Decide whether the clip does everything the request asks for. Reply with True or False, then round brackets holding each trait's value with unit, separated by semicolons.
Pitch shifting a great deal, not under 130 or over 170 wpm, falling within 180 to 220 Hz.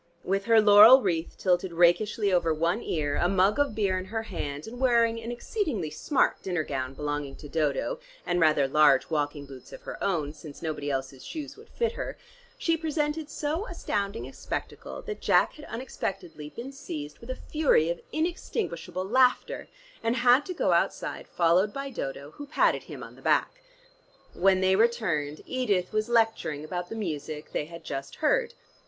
False (7.9 semitones; 180 wpm; 190 Hz)